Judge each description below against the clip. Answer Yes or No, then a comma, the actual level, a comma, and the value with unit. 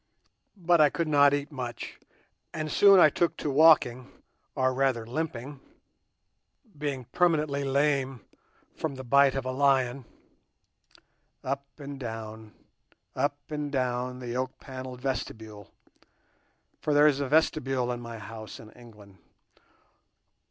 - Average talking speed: No, slow, 125 wpm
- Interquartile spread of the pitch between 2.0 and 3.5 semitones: Yes, average, 3.1 semitones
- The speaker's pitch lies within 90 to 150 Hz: Yes, low, 135 Hz